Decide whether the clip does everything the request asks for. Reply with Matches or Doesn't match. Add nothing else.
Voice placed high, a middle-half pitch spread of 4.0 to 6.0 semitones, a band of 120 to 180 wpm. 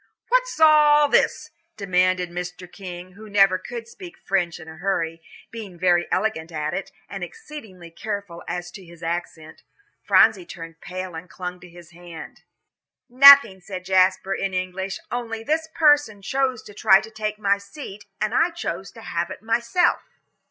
Matches